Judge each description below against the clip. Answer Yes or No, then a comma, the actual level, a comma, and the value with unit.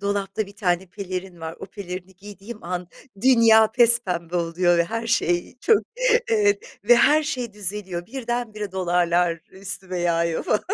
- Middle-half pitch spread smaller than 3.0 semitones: No, average, 4.5 semitones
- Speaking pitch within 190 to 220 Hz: Yes, high, 195 Hz